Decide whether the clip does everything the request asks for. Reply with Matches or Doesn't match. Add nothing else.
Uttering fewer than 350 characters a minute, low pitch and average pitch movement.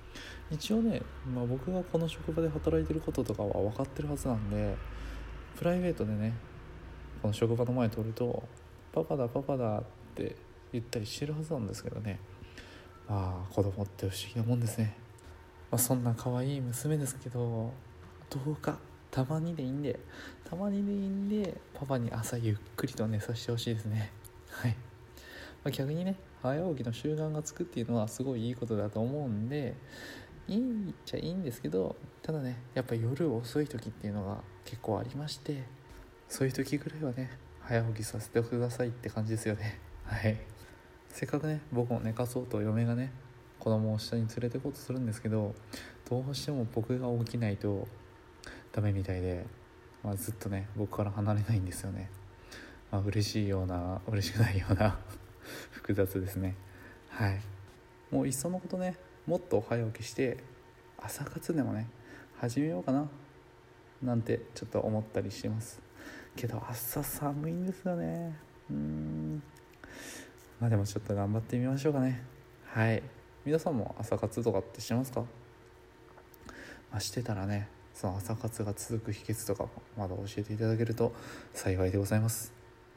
Matches